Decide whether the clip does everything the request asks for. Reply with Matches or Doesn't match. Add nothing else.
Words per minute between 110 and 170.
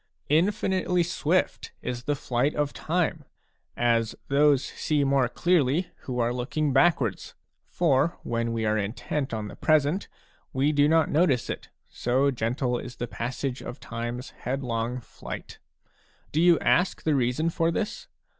Matches